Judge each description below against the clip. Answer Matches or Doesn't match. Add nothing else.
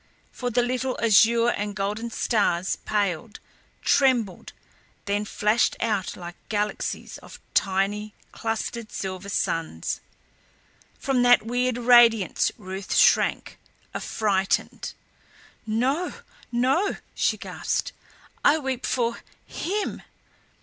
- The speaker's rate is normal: Doesn't match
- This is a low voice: Doesn't match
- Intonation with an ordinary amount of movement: Matches